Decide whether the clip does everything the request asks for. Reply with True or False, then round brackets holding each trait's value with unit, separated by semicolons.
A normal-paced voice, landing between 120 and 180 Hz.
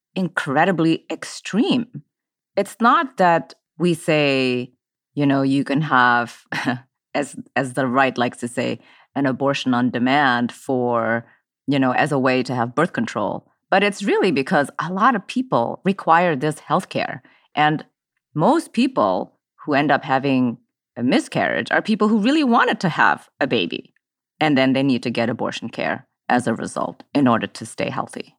True (165 wpm; 140 Hz)